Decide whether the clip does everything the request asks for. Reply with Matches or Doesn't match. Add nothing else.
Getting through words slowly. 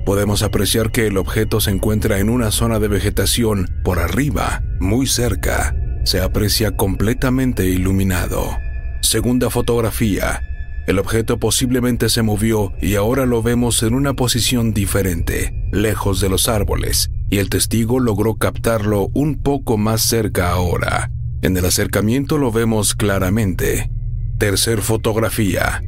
Matches